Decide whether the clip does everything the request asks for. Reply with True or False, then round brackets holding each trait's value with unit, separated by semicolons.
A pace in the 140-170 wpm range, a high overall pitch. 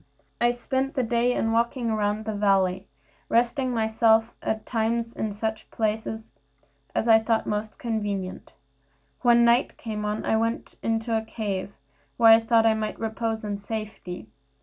True (160 wpm; 220 Hz)